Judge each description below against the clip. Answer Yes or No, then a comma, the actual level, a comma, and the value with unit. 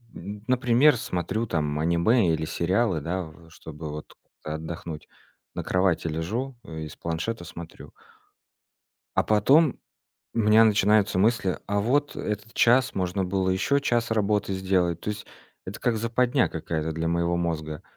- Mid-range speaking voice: No, very low, 95 Hz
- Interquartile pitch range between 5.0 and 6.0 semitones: Yes, wide, 5.4 semitones